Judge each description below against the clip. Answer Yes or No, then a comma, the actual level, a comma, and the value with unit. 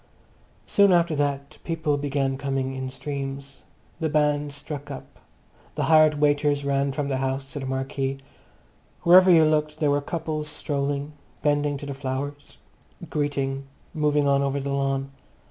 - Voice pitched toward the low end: No, medium, 145 Hz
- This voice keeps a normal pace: Yes, average, 150 wpm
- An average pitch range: No, narrow, 1.6 semitones